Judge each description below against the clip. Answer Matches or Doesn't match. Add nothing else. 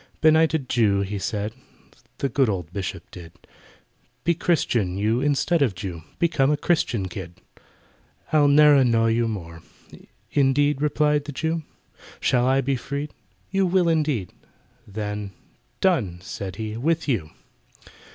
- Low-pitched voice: Matches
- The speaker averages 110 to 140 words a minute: Matches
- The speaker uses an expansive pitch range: Matches